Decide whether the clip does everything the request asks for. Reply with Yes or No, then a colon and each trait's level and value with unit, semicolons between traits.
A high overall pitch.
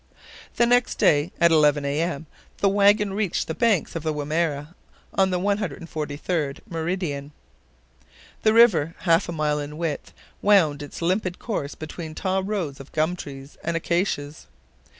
No: medium, 165 Hz